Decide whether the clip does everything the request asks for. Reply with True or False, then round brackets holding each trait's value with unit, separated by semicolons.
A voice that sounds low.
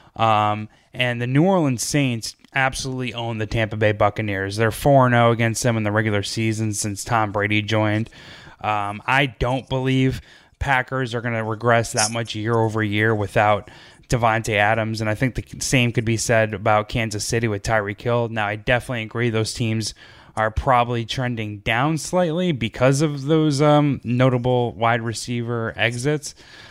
True (115 Hz)